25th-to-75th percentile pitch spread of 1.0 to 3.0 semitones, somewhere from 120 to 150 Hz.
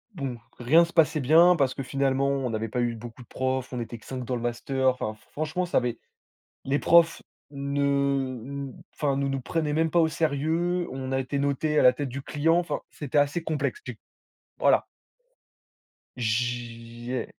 No: average, 3.6 semitones; low, 135 Hz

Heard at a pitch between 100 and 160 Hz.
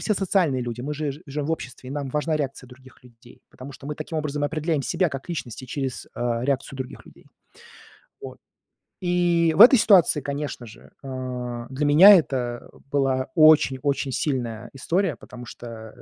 Yes: medium, 140 Hz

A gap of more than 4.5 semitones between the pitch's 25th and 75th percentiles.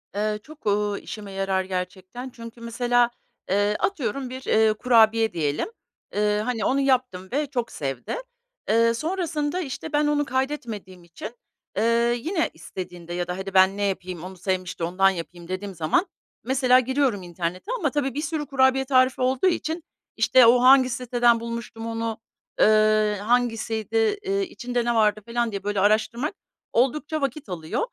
Yes: average, 5.1 semitones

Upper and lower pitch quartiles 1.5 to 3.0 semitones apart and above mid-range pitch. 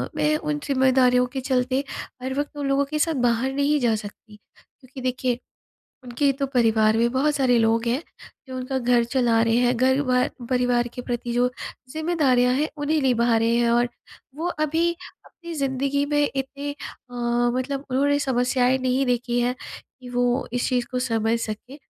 Yes: narrow, 2.5 semitones; very high, 255 Hz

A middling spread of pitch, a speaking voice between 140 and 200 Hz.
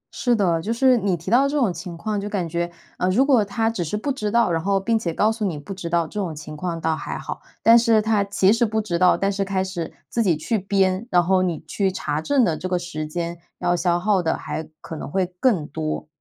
Yes: average, 4.2 semitones; high, 190 Hz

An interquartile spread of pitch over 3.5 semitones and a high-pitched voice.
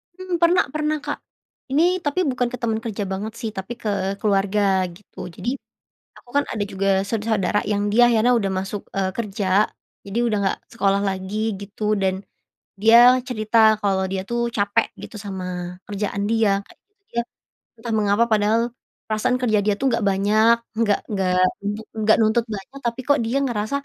No: average, 3.0 semitones; high, 215 Hz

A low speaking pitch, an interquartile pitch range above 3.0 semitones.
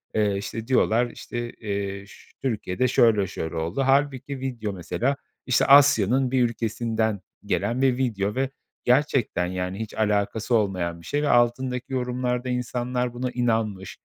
Yes: low, 120 Hz; average, 3.9 semitones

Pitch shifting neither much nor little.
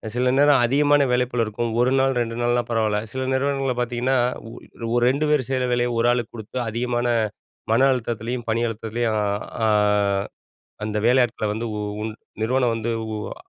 No: narrow, 2.3 semitones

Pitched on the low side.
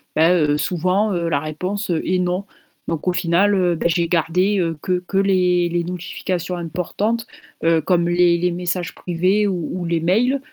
No: medium, 180 Hz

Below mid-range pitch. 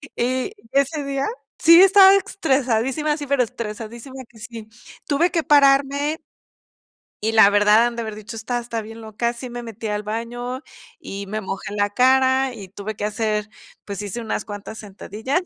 No: high, 235 Hz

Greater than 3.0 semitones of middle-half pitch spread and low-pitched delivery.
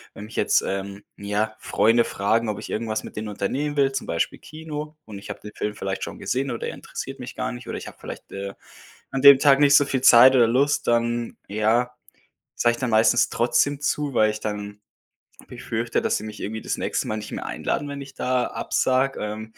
Yes: average, 4.0 semitones; low, 115 Hz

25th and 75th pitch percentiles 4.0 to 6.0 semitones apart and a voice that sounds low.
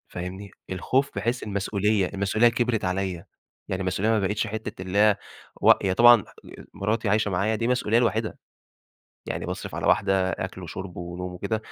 No: average, 2.9 semitones; low, 100 Hz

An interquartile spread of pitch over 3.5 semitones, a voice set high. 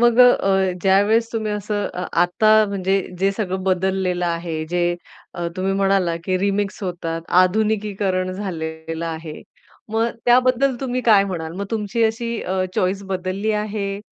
No: average, 3.1 semitones; high, 195 Hz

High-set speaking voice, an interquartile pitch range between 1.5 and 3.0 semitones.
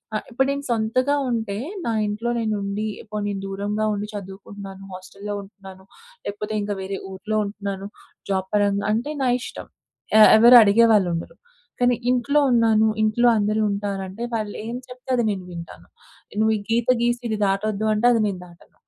Yes: high, 210 Hz; narrow, 2.6 semitones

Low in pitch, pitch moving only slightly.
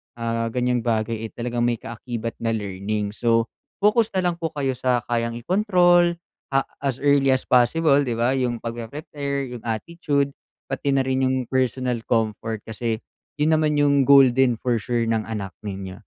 No: low, 125 Hz; average, 3.4 semitones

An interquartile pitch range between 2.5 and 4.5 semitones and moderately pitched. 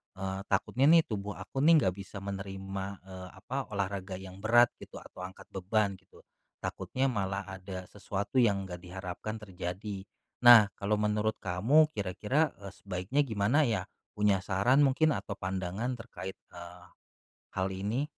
No: average, 3.2 semitones; low, 100 Hz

